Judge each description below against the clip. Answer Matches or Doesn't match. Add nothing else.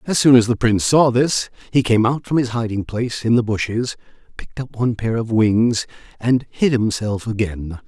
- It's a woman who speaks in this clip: Doesn't match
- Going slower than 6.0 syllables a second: Matches